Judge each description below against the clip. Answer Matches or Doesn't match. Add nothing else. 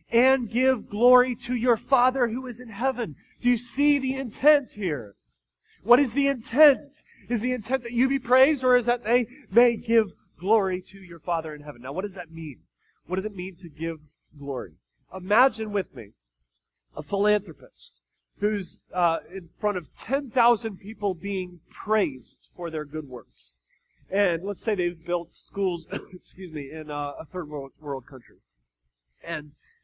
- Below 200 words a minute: Matches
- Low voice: Doesn't match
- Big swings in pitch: Matches